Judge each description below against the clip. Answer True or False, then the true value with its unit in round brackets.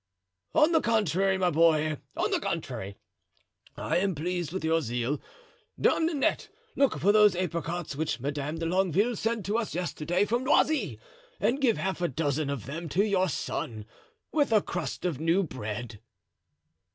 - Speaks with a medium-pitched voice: True (175 Hz)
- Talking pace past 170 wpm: False (165 wpm)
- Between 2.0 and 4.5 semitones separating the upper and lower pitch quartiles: False (5.5 semitones)